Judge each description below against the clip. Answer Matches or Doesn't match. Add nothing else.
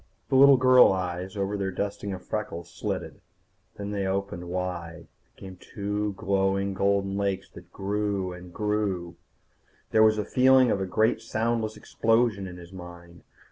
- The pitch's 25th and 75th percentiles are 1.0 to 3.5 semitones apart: Matches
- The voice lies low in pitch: Matches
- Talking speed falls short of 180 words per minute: Matches